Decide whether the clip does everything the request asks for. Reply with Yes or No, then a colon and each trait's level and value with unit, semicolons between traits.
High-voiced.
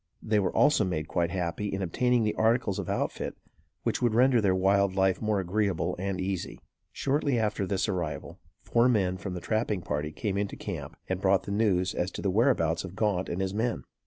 No: very low, 95 Hz